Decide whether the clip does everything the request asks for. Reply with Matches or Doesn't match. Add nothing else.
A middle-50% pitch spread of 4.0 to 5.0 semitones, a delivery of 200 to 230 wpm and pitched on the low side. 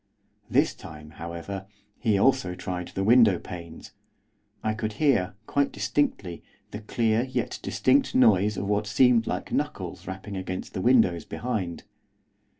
Doesn't match